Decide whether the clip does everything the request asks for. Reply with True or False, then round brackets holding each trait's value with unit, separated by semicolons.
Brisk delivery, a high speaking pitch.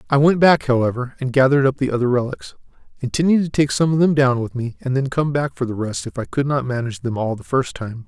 False (270 wpm; 130 Hz)